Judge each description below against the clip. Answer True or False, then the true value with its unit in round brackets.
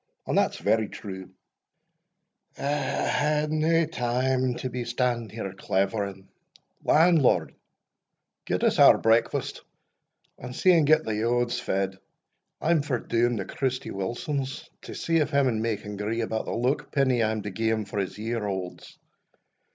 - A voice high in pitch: False (120 Hz)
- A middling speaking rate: True (160 wpm)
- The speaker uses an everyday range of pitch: True (4.4 semitones)